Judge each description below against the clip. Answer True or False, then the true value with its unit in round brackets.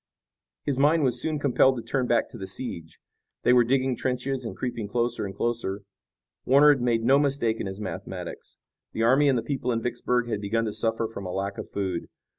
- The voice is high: False (120 Hz)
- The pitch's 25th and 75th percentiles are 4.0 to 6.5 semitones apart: False (3.0 semitones)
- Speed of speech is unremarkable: False (215 wpm)